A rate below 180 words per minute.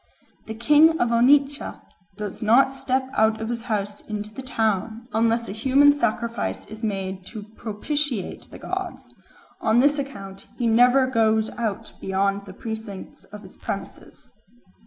Yes: average, 150 wpm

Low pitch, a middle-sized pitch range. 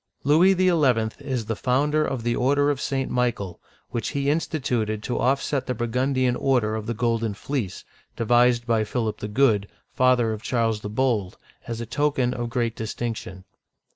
Yes: low, 120 Hz; average, 3.2 semitones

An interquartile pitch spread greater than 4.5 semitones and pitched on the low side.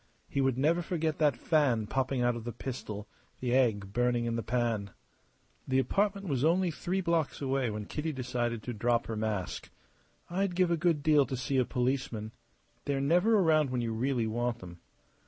Yes: average, 4.9 semitones; low, 130 Hz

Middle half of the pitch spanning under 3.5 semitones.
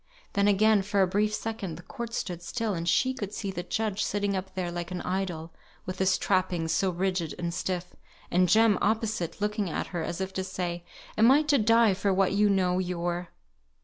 Yes: average, 3.0 semitones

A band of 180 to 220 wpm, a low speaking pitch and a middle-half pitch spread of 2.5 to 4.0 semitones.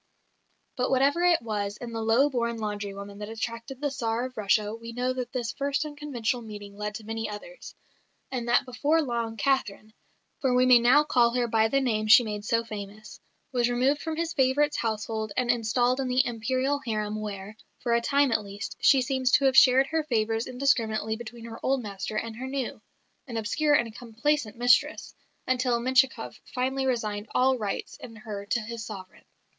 No: average, 190 wpm; high, 235 Hz; average, 3.2 semitones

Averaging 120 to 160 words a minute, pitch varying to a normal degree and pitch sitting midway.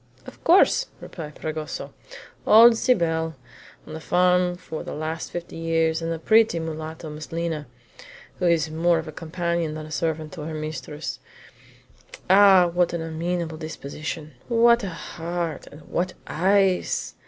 No: average, 150 wpm; narrow, 2.2 semitones; medium, 165 Hz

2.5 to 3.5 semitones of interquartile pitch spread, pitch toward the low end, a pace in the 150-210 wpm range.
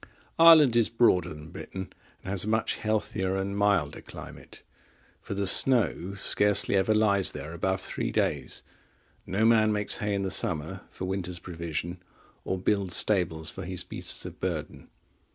Yes: average, 2.8 semitones; very low, 95 Hz; average, 165 wpm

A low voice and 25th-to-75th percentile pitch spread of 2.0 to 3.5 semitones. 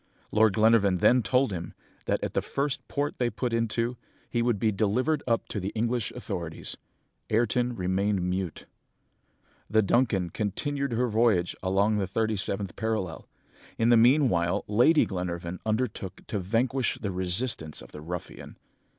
No: low, 110 Hz; average, 4.2 semitones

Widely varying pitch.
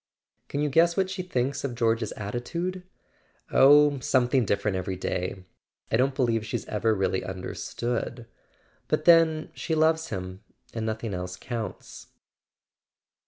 Yes: wide, 5.9 semitones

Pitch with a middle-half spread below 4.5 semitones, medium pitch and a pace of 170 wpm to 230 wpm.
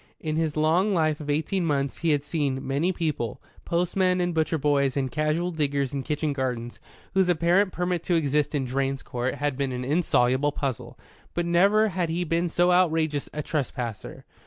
Yes: average, 3.8 semitones; medium, 155 Hz; average, 180 wpm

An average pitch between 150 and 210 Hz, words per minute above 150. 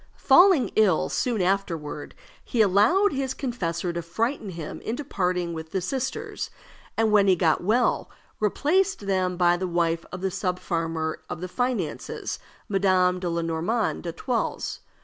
No: medium, 185 Hz; average, 145 wpm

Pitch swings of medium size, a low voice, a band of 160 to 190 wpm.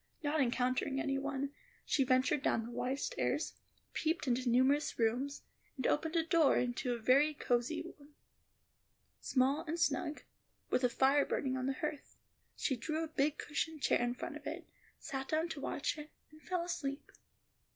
No: average, 3.1 semitones; very high, 275 Hz; average, 170 wpm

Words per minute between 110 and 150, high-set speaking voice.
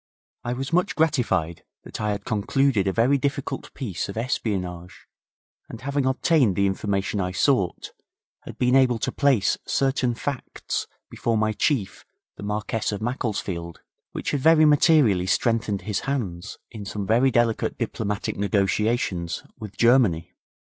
No: average, 145 wpm; low, 110 Hz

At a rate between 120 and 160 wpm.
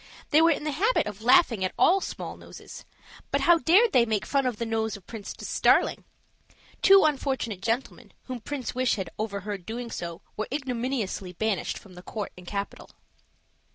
No: average, 180 wpm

